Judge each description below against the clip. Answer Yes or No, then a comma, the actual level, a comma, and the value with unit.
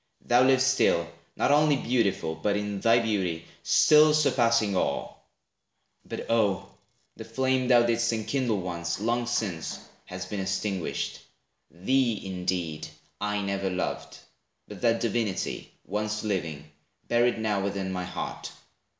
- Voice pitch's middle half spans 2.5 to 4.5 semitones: Yes, average, 4.2 semitones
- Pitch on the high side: No, low, 105 Hz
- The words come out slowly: Yes, slow, 130 wpm